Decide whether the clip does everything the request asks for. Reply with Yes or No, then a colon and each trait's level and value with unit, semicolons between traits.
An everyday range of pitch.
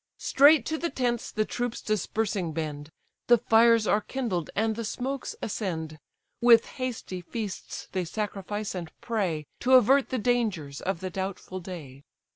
Yes: average, 4.9 semitones